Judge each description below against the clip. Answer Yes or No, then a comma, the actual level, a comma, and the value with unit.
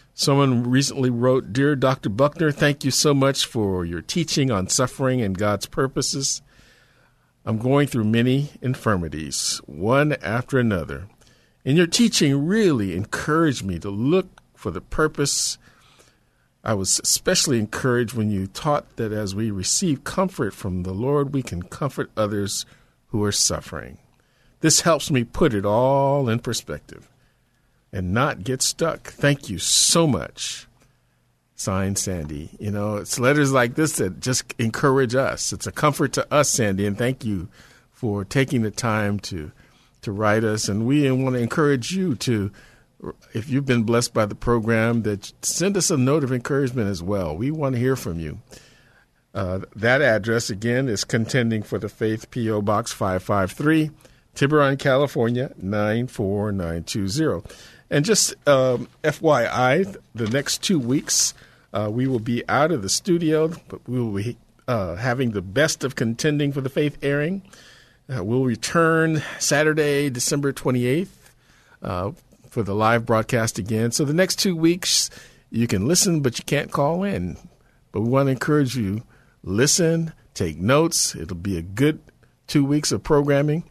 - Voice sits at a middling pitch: No, low, 125 Hz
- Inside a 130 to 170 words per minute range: Yes, average, 160 wpm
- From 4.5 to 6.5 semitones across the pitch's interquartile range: Yes, average, 5.2 semitones